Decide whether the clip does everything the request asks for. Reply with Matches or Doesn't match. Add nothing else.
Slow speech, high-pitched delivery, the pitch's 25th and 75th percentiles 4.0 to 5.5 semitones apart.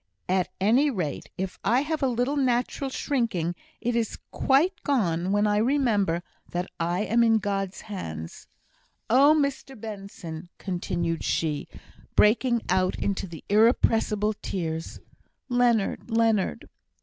Matches